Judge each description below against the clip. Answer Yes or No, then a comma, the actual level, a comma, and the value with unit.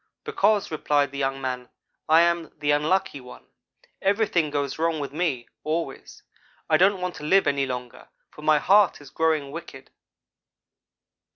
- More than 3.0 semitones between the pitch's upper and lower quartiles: Yes, average, 3.8 semitones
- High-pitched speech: No, medium, 155 Hz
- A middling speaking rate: Yes, average, 155 wpm